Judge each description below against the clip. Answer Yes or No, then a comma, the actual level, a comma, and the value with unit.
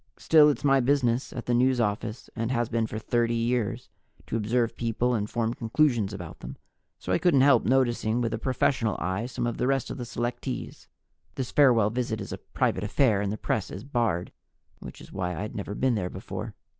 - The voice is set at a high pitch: No, low, 120 Hz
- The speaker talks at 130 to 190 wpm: No, fast, 205 wpm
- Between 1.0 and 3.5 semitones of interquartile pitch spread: Yes, average, 2.7 semitones